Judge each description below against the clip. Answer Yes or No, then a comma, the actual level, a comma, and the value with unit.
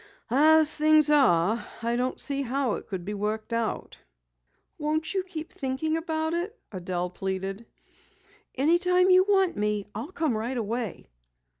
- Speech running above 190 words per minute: No, average, 145 wpm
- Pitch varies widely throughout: Yes, wide, 6.9 semitones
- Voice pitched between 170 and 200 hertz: No, very high, 270 Hz